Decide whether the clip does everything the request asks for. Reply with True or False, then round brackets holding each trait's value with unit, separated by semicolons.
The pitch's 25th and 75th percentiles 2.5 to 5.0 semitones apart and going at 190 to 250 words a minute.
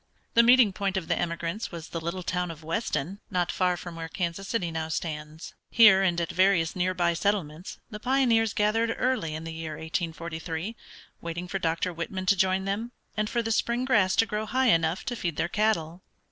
True (4.2 semitones; 200 wpm)